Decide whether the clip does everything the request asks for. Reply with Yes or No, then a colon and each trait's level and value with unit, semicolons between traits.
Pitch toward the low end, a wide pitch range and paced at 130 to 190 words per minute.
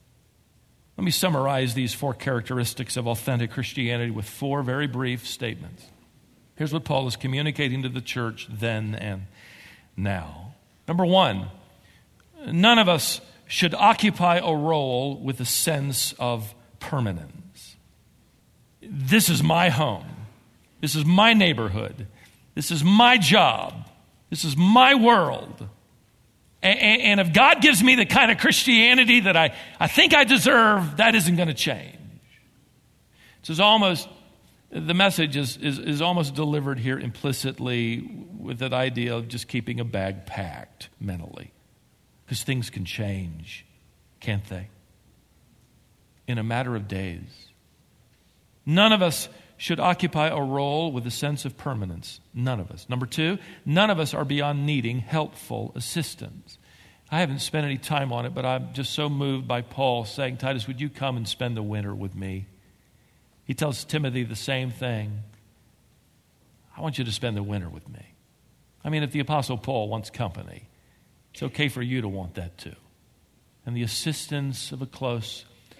Yes: low, 130 Hz; wide, 5.7 semitones; average, 155 wpm